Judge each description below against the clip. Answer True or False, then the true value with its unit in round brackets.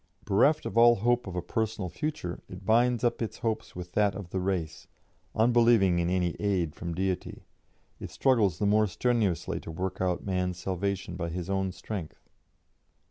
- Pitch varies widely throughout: False (3.8 semitones)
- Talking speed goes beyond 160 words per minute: True (175 wpm)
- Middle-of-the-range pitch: False (95 Hz)